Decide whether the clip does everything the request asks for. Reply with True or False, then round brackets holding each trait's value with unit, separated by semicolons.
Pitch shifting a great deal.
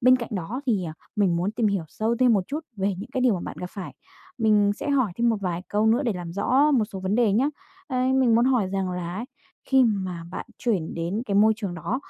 False (4.7 semitones)